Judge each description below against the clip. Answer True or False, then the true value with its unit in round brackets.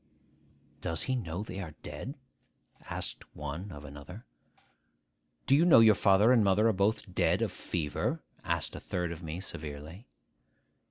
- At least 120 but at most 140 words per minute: False (155 wpm)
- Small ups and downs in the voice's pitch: False (5.3 semitones)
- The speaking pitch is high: False (95 Hz)